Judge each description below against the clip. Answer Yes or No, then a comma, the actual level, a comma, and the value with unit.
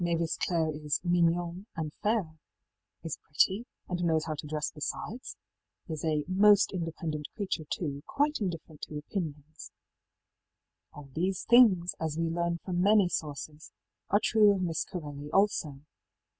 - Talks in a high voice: No, medium, 165 Hz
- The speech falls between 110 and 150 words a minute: Yes, average, 145 wpm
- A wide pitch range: No, average, 3.5 semitones